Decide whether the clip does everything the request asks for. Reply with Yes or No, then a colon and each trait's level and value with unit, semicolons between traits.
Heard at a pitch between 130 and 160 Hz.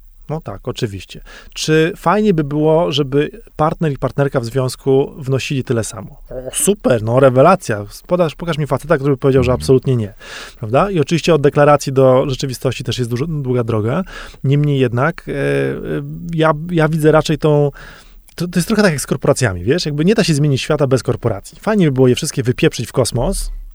Yes: medium, 140 Hz